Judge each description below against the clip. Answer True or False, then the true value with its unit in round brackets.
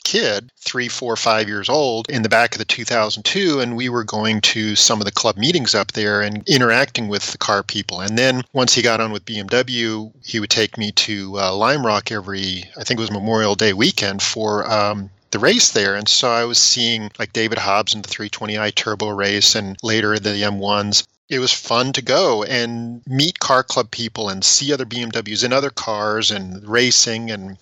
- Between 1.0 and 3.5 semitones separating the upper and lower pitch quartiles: True (2.5 semitones)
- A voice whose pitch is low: True (110 Hz)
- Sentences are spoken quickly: True (210 wpm)